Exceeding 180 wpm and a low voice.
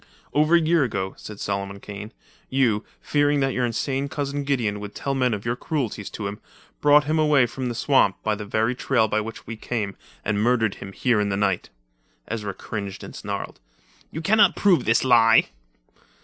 Yes: average, 195 wpm; low, 115 Hz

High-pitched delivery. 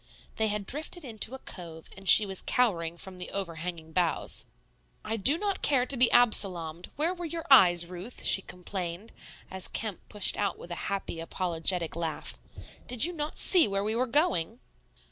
Yes: high, 195 Hz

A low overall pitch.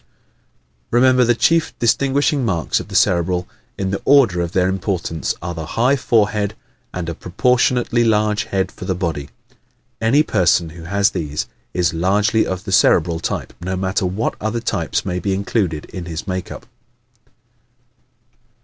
Yes: very low, 95 Hz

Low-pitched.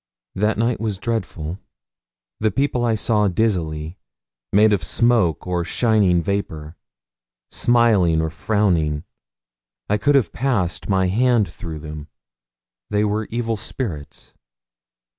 Yes: low, 100 Hz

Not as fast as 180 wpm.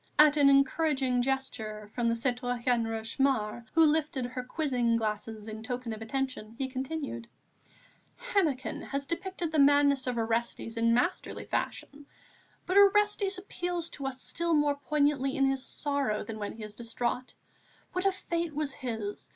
Yes: average, 155 wpm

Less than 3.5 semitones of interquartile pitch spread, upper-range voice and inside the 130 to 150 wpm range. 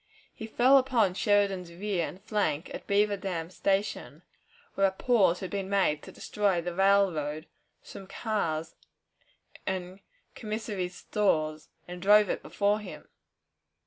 Yes: average, 2.8 semitones; high, 195 Hz; slow, 135 wpm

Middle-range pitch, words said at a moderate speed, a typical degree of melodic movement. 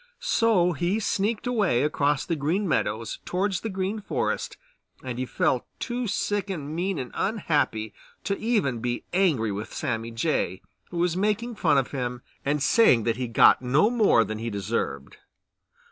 No: medium, 155 Hz; average, 170 wpm; wide, 8.6 semitones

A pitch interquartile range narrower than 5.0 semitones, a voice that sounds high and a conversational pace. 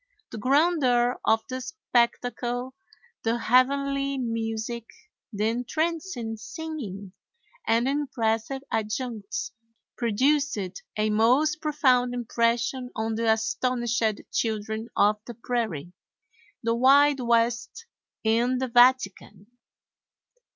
No: average, 2.8 semitones; high, 240 Hz; slow, 95 wpm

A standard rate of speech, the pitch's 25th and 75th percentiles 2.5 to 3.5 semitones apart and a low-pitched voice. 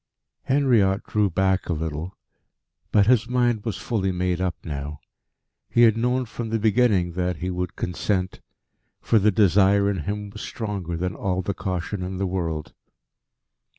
Yes: average, 160 wpm; average, 3.1 semitones; very low, 95 Hz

